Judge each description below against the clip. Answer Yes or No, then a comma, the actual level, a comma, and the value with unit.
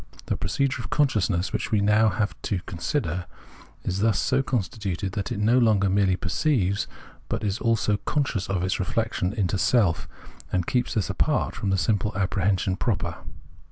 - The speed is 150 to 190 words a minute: Yes, average, 165 wpm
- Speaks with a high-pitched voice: No, low, 100 Hz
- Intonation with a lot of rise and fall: No, average, 3.4 semitones